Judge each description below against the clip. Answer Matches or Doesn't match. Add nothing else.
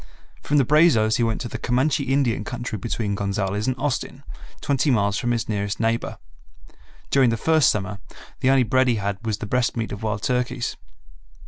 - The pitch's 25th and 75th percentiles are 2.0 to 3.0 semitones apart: Doesn't match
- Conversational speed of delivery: Matches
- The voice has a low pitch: Matches